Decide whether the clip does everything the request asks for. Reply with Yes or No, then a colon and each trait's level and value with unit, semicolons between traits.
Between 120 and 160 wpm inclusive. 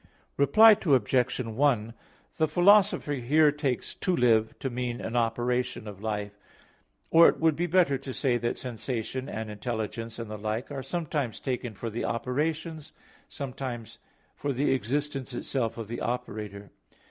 Yes: average, 150 wpm